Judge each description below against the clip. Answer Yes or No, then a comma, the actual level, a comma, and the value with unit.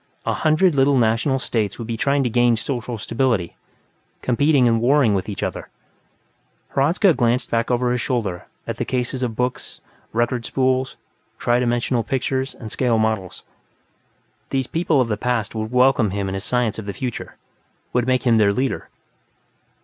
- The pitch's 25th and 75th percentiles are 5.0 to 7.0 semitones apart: No, average, 2.8 semitones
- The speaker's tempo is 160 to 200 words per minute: Yes, average, 170 wpm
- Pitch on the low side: Yes, low, 120 Hz